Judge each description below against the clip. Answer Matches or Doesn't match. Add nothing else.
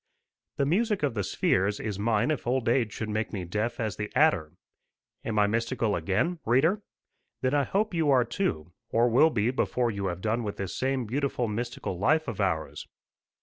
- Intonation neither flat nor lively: Matches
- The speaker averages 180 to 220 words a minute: Matches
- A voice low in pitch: Matches